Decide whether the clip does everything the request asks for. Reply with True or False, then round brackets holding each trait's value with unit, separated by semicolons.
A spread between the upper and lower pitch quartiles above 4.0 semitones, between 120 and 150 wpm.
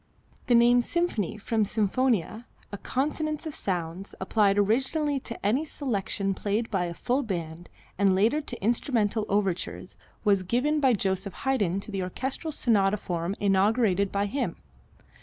True (4.6 semitones; 145 wpm)